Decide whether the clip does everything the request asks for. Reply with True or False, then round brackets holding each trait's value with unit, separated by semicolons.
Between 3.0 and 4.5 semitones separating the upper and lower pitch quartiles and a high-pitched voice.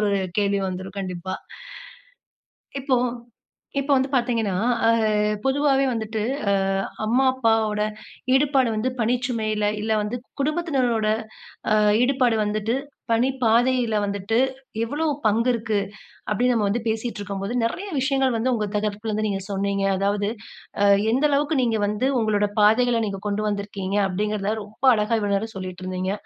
True (3.5 semitones; 220 Hz)